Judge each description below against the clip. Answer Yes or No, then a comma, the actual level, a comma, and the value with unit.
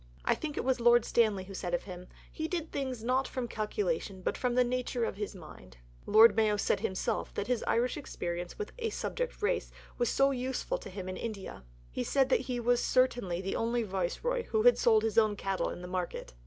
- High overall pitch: Yes, high, 235 Hz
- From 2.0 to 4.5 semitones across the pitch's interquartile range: No, average, 5.3 semitones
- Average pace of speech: No, fast, 220 wpm